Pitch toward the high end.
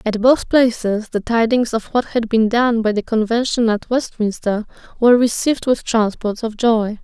Yes: high, 230 Hz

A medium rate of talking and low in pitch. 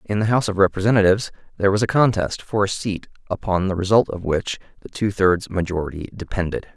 Yes: average, 195 wpm; low, 100 Hz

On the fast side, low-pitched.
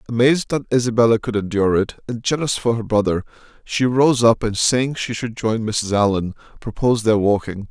No: average, 185 wpm; low, 115 Hz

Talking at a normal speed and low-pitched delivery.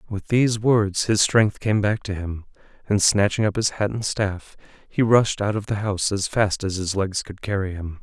No: fast, 225 wpm; low, 100 Hz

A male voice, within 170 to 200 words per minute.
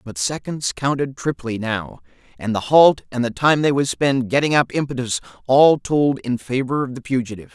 Yes: male; average, 190 wpm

